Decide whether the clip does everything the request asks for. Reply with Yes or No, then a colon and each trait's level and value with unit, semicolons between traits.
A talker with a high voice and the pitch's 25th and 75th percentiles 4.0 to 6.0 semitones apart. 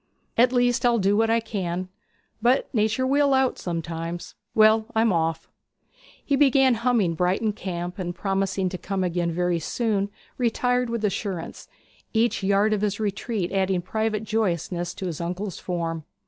Yes: high, 200 Hz; average, 4.4 semitones